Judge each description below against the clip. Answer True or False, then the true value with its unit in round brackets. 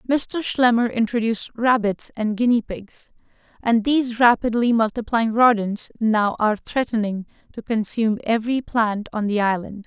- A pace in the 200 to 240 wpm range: False (135 wpm)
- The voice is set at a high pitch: True (225 Hz)